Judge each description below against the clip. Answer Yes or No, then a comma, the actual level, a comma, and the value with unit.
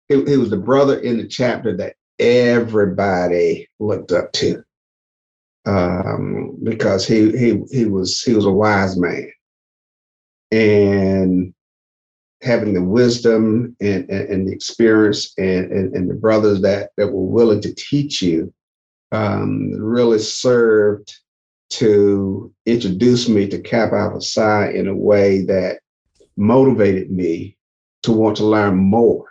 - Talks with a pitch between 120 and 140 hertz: No, low, 105 Hz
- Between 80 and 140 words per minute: Yes, slow, 135 wpm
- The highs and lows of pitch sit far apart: No, average, 3.0 semitones